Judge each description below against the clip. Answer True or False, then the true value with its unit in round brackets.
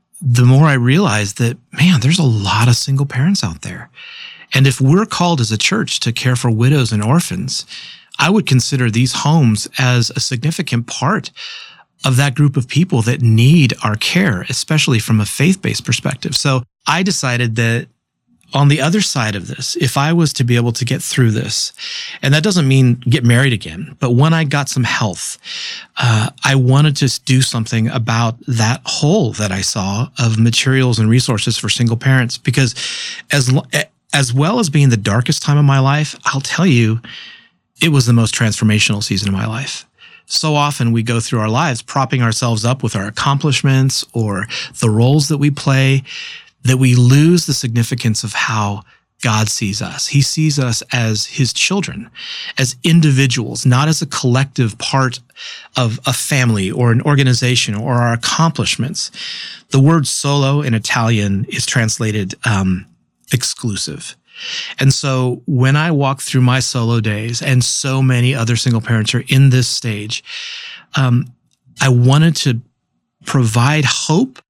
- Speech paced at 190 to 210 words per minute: False (170 wpm)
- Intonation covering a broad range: False (3.5 semitones)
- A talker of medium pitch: False (130 Hz)